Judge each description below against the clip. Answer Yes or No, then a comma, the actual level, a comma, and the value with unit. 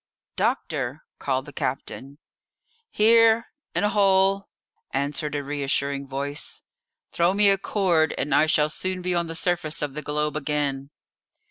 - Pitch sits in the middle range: Yes, medium, 155 Hz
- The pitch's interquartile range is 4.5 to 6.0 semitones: Yes, average, 5.0 semitones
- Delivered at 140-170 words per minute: Yes, average, 145 wpm